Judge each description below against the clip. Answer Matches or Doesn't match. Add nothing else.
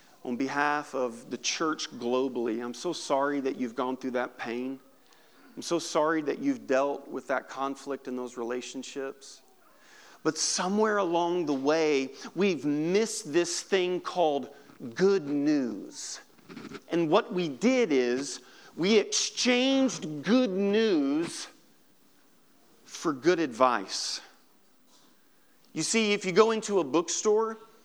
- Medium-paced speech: Doesn't match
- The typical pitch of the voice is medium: Matches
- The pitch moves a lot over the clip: Matches